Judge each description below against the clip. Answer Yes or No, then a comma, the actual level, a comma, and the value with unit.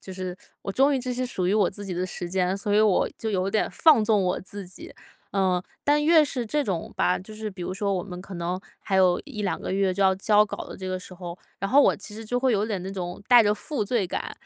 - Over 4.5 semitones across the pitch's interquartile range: No, average, 3.0 semitones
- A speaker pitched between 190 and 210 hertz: Yes, high, 195 Hz